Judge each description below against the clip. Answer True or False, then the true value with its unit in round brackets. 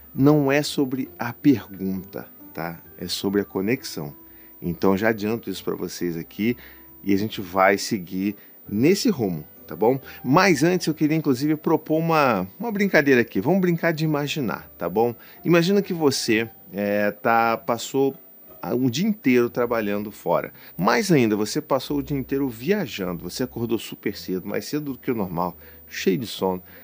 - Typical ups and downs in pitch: False (7.3 semitones)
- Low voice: True (120 Hz)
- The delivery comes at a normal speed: True (165 wpm)